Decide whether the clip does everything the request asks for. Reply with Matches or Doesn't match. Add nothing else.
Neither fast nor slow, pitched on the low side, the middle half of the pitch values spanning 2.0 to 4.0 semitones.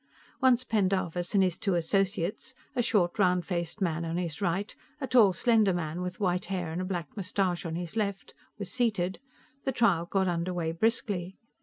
Doesn't match